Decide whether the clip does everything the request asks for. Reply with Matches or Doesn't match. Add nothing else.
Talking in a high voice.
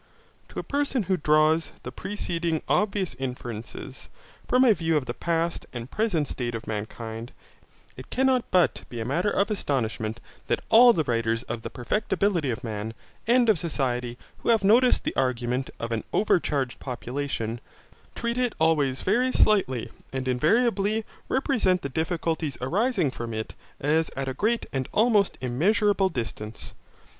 Doesn't match